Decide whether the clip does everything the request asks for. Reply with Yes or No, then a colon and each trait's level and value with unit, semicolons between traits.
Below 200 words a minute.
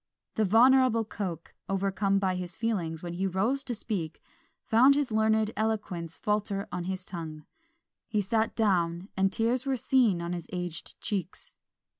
Yes: average, 155 wpm